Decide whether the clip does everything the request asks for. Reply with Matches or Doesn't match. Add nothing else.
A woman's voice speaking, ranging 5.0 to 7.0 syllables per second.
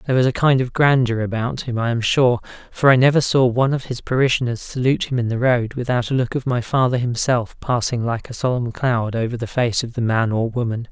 Doesn't match